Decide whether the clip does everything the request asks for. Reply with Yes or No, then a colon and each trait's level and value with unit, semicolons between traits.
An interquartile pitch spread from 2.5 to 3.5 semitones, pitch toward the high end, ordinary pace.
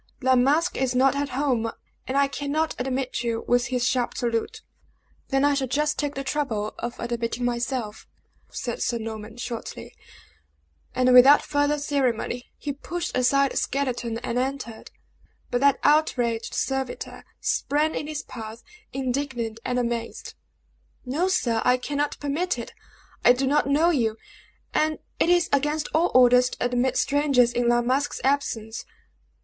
Yes: average, 3.1 semitones; very high, 260 Hz; average, 155 wpm